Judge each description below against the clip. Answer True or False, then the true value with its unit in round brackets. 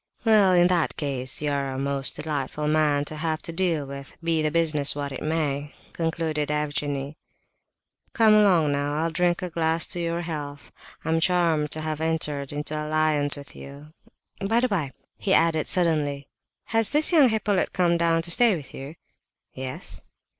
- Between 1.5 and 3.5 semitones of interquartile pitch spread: True (3.0 semitones)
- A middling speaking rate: True (175 wpm)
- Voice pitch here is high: False (155 Hz)